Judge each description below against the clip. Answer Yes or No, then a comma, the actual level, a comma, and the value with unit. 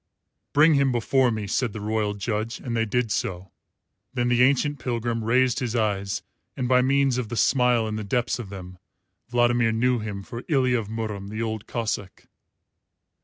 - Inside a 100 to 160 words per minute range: No, average, 180 wpm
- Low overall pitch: Yes, low, 115 Hz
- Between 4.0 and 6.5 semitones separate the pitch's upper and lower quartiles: No, average, 2.7 semitones